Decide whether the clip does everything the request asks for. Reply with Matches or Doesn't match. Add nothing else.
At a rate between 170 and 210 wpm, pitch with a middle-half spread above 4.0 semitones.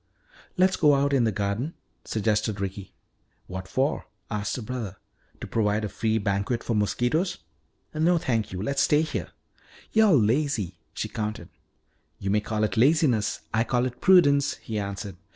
Doesn't match